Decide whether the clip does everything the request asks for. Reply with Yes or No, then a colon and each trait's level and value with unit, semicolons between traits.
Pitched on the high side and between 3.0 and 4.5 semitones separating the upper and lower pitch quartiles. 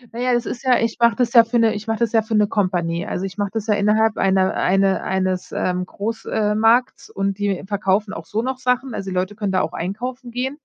Yes: high, 210 Hz; average, 3.4 semitones